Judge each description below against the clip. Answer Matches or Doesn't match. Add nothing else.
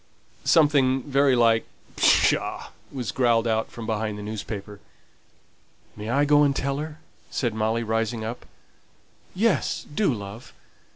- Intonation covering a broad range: Doesn't match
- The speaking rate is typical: Doesn't match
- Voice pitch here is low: Matches